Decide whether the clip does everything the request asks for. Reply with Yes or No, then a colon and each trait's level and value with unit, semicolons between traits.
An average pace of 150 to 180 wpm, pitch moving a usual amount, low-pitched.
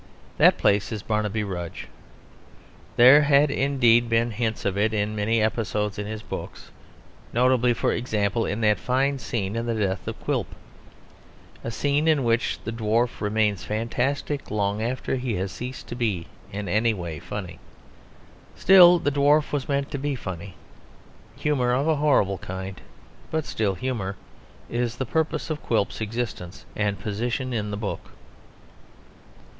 Yes: average, 155 wpm; average, 4.0 semitones; low, 115 Hz